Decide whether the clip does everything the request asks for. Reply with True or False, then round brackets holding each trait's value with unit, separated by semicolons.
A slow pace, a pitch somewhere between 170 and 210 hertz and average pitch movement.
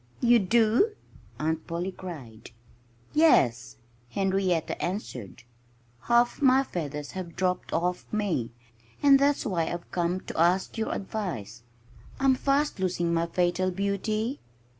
True (120 wpm; 185 Hz; 5.0 semitones)